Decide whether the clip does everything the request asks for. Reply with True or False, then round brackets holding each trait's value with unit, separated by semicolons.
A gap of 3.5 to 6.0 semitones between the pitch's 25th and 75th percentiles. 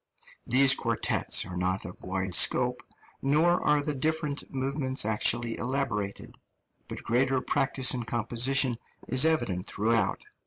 True (3.8 semitones)